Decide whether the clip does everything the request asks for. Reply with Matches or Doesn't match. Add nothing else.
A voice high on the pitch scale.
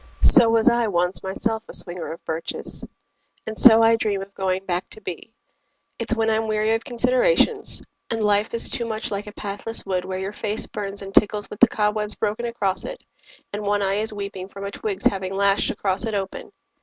Matches